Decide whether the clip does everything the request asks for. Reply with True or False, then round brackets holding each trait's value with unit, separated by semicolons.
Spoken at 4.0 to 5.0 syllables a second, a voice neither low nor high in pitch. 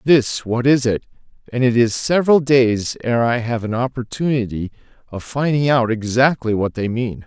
False (4.6 syllables/s; 120 Hz)